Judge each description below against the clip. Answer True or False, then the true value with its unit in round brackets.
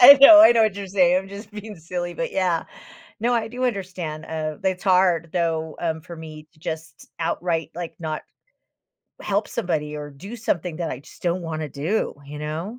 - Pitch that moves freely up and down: False (4.0 semitones)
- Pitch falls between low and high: True (175 Hz)